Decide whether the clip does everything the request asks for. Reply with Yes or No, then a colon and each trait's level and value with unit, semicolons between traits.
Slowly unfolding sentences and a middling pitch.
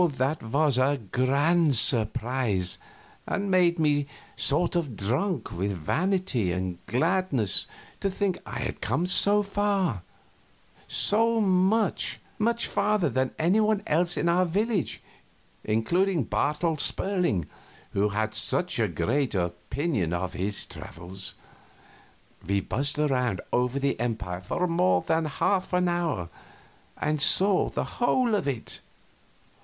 Yes: slow, 125 wpm; medium, 145 Hz